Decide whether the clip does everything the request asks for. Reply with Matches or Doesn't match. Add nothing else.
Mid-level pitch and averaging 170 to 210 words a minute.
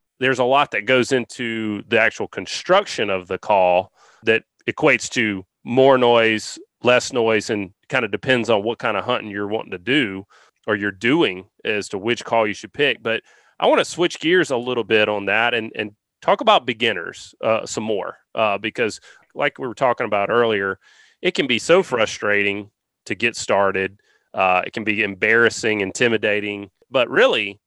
Doesn't match